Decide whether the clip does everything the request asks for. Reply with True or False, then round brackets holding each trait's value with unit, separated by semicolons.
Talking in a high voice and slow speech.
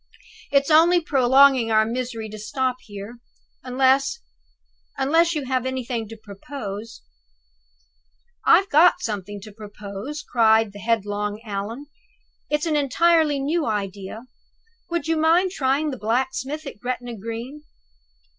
True (255 Hz; 125 wpm)